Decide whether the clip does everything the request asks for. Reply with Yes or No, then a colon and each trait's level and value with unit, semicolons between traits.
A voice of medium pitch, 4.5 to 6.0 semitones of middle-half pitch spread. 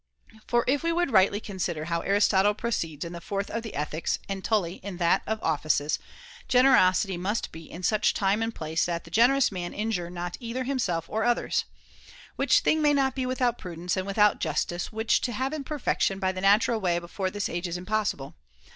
No: high, 195 Hz; average, 5.0 semitones